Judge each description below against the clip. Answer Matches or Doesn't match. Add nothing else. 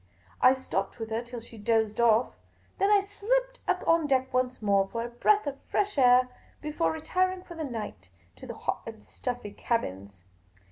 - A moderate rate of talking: Matches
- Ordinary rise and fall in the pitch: Doesn't match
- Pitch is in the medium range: Doesn't match